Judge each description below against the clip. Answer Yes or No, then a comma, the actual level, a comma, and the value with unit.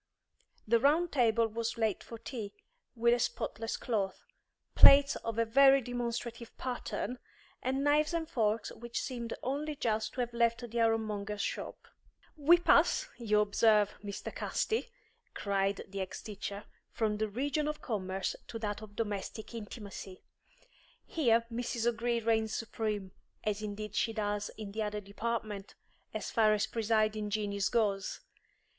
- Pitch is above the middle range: Yes, high, 225 Hz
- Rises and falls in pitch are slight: Yes, narrow, 2.3 semitones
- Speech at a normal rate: Yes, average, 145 wpm